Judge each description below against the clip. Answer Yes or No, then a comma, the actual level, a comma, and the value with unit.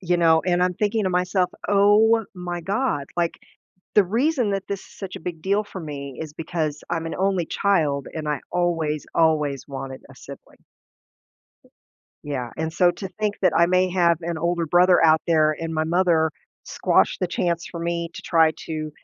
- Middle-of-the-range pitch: Yes, medium, 170 Hz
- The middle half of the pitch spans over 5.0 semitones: No, average, 2.8 semitones